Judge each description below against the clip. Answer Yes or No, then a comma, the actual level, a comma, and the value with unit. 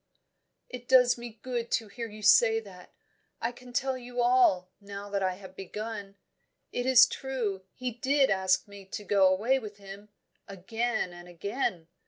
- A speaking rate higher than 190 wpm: No, average, 170 wpm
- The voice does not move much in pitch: No, average, 3.9 semitones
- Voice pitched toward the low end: No, high, 215 Hz